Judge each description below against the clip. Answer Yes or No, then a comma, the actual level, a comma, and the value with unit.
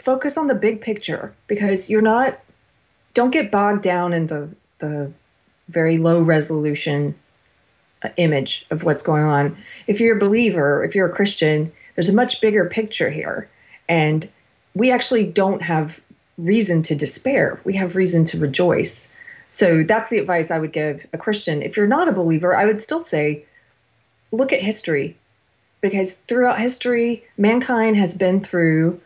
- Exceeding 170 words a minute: No, average, 160 wpm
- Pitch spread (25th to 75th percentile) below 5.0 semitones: No, wide, 5.5 semitones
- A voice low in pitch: No, medium, 185 Hz